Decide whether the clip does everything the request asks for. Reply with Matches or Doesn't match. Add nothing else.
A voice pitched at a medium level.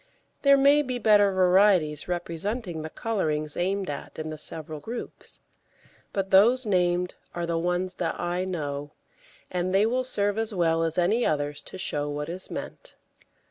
Matches